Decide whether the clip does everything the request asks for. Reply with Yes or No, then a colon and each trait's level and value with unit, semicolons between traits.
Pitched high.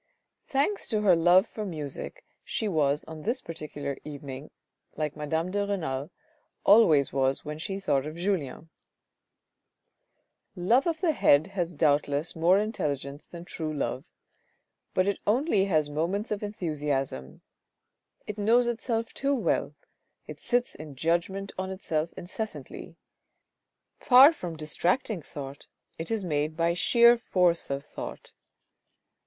No: medium, 170 Hz